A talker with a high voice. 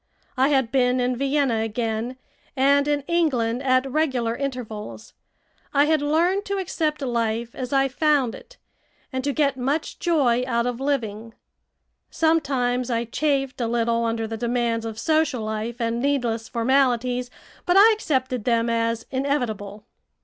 Yes: very high, 250 Hz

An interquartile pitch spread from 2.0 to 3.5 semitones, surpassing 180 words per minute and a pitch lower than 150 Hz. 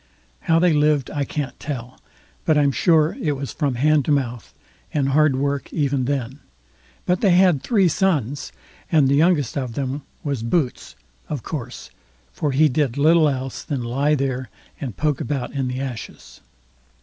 No: average, 2.8 semitones; average, 170 wpm; medium, 140 Hz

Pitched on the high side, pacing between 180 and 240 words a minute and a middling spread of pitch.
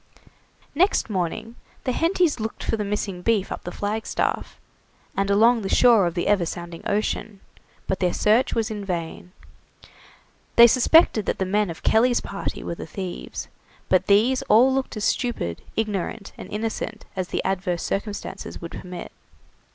No: high, 205 Hz; average, 160 wpm; average, 3.7 semitones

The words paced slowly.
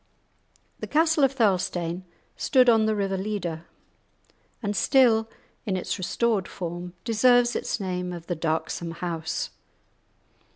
Yes: slow, 125 wpm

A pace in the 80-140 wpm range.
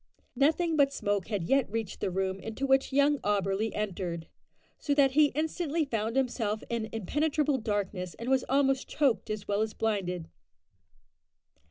No: average, 155 wpm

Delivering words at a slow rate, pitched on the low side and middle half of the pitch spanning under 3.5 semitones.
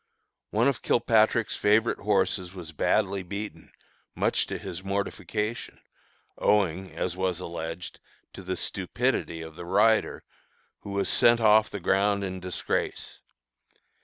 Yes: slow, 130 wpm; low, 100 Hz; average, 2.9 semitones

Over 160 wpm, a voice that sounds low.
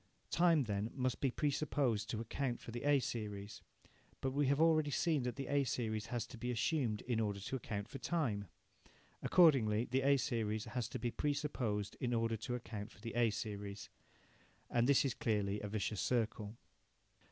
Yes: average, 190 wpm; low, 120 Hz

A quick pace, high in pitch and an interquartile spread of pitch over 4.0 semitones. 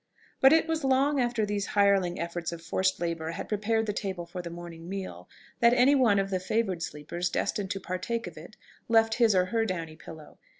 Yes: fast, 210 wpm; high, 195 Hz; average, 4.7 semitones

